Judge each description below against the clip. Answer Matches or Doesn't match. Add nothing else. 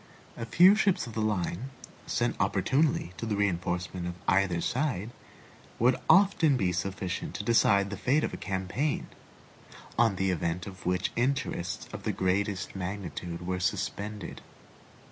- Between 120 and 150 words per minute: Matches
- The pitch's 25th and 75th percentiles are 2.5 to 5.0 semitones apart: Matches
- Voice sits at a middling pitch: Doesn't match